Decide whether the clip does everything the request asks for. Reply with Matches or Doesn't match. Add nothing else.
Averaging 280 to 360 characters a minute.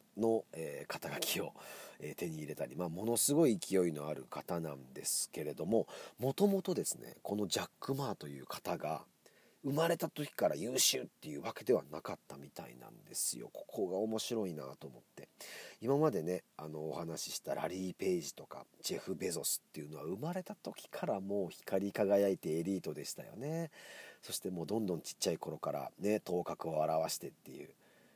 Doesn't match